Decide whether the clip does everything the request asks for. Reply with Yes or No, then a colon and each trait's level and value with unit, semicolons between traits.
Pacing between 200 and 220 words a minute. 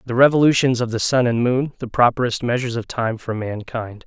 Yes: fast, 205 wpm